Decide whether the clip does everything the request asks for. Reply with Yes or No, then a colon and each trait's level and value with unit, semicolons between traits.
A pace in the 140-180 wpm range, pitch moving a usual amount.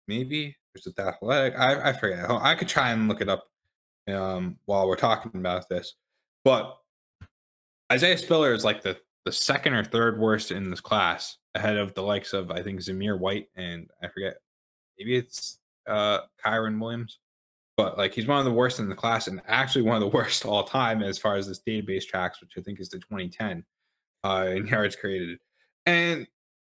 No: average, 195 wpm; average, 3.8 semitones